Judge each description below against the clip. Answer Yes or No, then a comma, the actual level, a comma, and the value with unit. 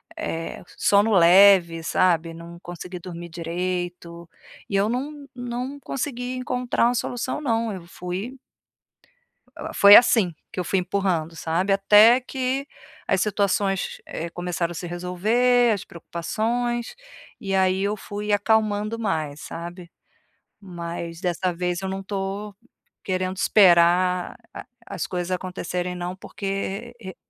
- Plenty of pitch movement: No, average, 3.8 semitones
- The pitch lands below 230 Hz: Yes, high, 190 Hz